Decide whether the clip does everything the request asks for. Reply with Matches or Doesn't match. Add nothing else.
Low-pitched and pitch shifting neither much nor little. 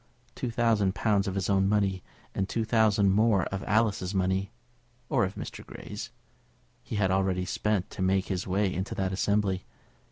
Doesn't match